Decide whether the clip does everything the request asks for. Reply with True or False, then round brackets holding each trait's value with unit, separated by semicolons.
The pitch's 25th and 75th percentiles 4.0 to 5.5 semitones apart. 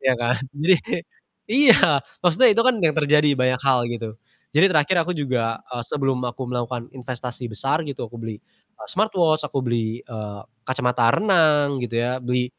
True (4.4 semitones)